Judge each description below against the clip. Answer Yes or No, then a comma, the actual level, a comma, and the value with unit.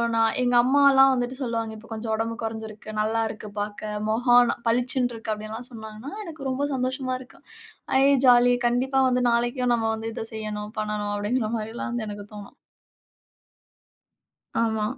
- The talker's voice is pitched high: Yes, high, 230 Hz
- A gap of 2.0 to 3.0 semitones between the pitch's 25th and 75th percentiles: Yes, narrow, 2.5 semitones